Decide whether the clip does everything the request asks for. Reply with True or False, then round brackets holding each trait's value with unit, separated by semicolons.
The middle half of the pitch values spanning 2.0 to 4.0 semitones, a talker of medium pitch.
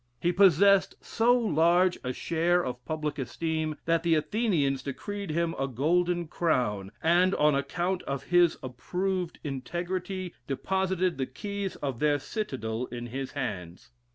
False (5.2 semitones; 165 Hz)